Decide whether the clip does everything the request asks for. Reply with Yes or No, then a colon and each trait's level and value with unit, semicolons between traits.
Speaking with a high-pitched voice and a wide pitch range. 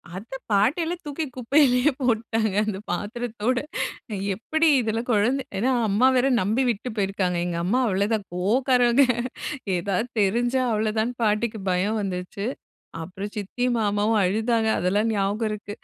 No: high, 220 Hz; average, 3.5 semitones